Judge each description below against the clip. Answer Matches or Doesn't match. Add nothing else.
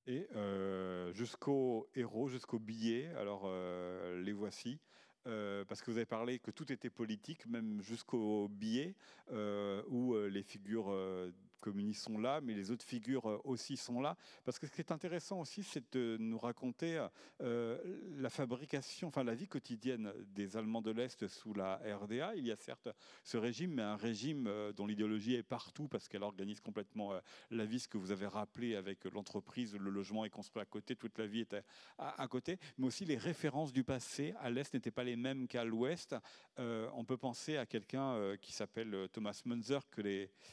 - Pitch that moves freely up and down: Doesn't match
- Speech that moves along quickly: Doesn't match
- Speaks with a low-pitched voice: Matches